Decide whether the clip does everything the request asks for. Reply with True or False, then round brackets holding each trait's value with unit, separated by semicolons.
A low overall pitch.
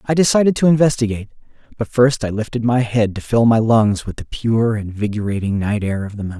True (115 Hz)